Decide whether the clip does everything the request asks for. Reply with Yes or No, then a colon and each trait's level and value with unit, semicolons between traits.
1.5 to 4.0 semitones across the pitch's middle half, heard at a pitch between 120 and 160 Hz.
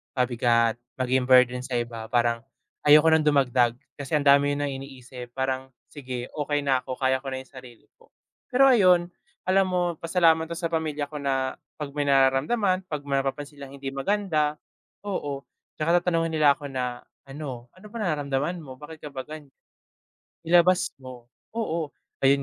Yes: average, 3.6 semitones; medium, 140 Hz